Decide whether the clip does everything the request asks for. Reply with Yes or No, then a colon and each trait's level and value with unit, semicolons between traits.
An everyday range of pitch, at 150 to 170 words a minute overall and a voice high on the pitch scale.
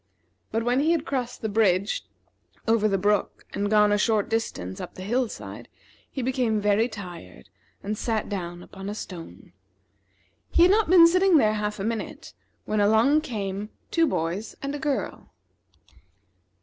Yes: average, 4.4 semitones; average, 165 wpm; high, 215 Hz